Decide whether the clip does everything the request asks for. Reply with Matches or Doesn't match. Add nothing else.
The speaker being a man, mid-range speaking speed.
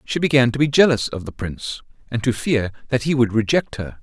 Doesn't match